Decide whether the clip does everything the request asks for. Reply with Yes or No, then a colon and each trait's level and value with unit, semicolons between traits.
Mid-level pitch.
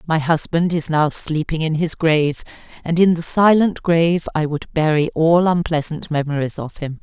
Yes: medium, 160 Hz